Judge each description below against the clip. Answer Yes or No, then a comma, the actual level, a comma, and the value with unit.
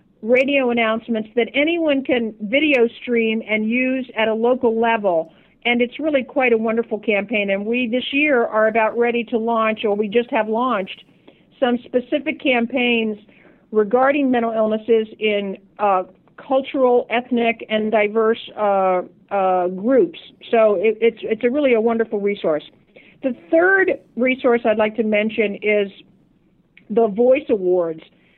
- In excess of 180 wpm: No, average, 145 wpm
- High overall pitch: Yes, high, 230 Hz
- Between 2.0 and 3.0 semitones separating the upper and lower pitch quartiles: Yes, average, 2.7 semitones